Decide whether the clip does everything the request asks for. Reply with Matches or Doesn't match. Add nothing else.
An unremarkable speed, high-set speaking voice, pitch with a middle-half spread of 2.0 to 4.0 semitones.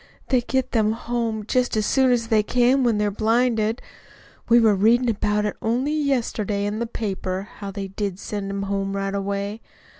Matches